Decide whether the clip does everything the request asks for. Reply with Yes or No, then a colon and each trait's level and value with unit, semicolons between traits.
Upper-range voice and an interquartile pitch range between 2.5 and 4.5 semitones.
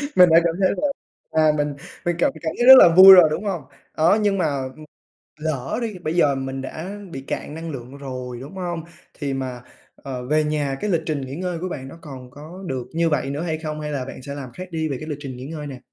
No: medium, 150 Hz; average, 4.0 semitones